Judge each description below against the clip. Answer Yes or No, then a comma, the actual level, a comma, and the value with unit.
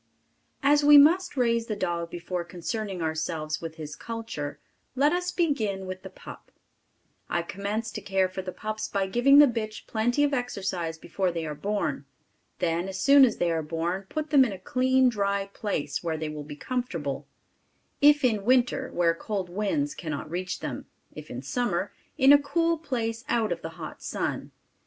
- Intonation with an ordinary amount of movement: No, wide, 6.9 semitones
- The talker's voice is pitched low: No, high, 200 Hz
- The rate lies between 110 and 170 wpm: No, average, 185 wpm